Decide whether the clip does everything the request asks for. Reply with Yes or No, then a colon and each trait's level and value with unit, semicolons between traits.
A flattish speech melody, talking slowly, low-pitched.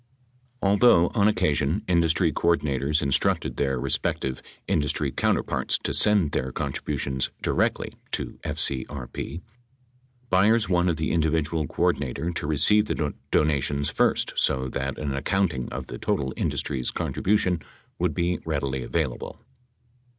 No: average, 4.3 semitones; slow, 125 wpm; very low, 75 Hz